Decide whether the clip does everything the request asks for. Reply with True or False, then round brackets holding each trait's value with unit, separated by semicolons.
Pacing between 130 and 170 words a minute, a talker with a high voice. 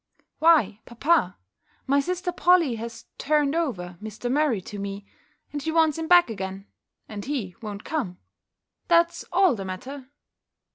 True (145 wpm; 265 Hz)